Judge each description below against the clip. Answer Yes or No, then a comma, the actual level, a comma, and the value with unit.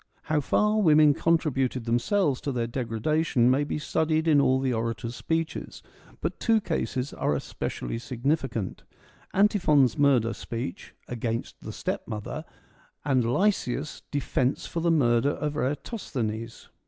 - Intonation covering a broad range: No, average, 4.9 semitones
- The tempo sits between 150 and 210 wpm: No, slow, 135 wpm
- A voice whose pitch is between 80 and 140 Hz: Yes, low, 135 Hz